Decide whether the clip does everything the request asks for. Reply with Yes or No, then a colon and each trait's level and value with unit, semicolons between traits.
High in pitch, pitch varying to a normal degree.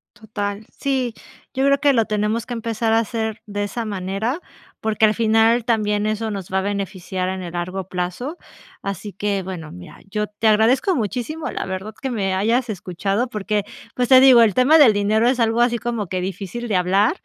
Yes: high, 215 Hz; average, 3.2 semitones